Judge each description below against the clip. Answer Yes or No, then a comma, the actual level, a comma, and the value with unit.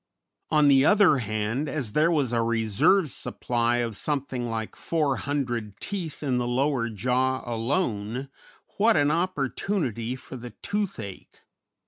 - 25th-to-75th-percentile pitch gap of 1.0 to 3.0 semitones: No, average, 4.5 semitones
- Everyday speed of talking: No, slow, 130 wpm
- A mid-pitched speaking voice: No, low, 130 Hz